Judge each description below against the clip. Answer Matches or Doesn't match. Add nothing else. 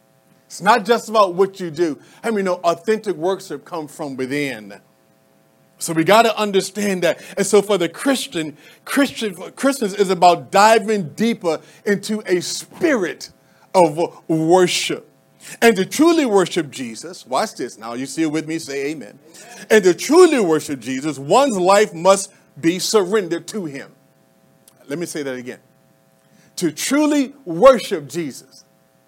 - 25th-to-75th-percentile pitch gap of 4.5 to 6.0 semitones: Matches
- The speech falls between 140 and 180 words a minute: Matches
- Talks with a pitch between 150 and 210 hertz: Matches